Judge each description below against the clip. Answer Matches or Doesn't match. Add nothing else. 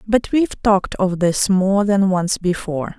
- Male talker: Doesn't match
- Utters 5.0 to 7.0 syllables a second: Doesn't match